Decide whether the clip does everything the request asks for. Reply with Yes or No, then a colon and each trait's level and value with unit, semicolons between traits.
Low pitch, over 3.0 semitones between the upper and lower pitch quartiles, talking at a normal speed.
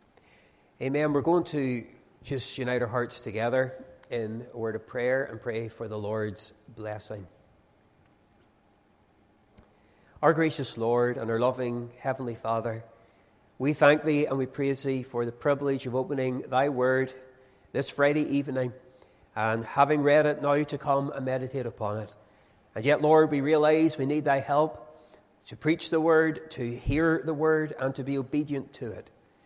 Yes: low, 130 Hz; average, 4.2 semitones; average, 160 wpm